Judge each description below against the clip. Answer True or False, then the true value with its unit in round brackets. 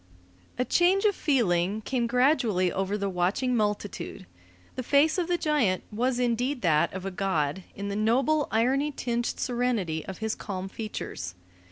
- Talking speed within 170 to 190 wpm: False (160 wpm)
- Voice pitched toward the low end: False (225 Hz)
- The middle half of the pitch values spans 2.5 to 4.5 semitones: False (5.3 semitones)